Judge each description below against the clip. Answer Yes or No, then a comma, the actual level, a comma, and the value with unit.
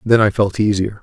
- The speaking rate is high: Yes, fast, 235 wpm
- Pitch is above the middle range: No, low, 105 Hz